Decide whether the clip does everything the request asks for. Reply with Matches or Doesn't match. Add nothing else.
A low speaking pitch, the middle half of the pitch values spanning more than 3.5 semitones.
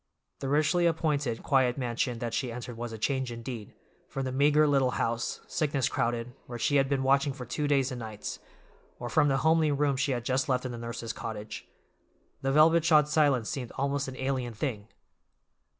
Doesn't match